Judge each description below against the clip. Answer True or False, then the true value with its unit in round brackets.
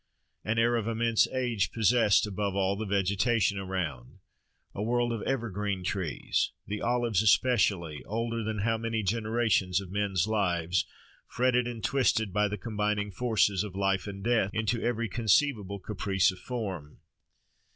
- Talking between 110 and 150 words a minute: True (140 wpm)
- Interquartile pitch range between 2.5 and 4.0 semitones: True (3.1 semitones)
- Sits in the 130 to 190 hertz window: False (105 Hz)